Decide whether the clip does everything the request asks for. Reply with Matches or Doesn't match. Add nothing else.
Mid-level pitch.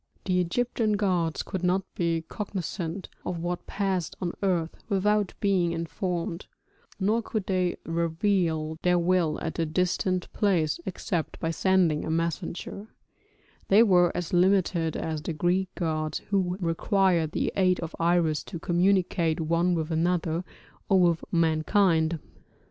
Matches